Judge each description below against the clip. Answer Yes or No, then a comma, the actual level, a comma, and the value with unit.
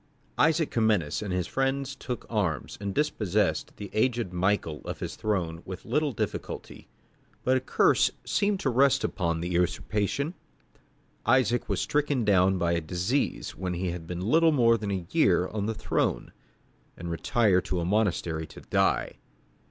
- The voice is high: No, low, 105 Hz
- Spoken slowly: No, average, 160 wpm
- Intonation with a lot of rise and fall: Yes, wide, 6.4 semitones